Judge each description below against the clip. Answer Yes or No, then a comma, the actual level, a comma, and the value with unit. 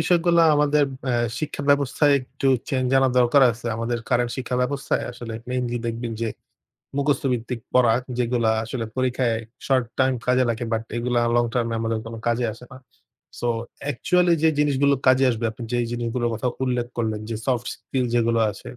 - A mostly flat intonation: Yes, narrow, 2.2 semitones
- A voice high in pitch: No, low, 125 Hz